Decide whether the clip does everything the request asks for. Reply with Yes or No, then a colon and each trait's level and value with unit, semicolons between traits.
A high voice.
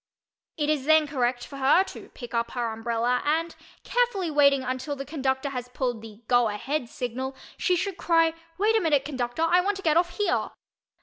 Yes: very high, 280 Hz